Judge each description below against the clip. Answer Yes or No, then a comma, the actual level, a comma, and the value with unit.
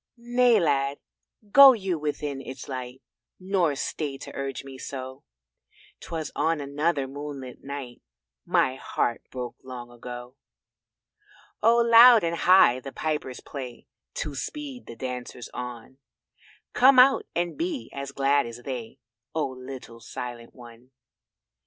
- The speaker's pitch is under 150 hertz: Yes, medium, 140 Hz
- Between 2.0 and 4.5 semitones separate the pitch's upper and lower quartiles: No, average, 5.1 semitones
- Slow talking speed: Yes, slow, 130 wpm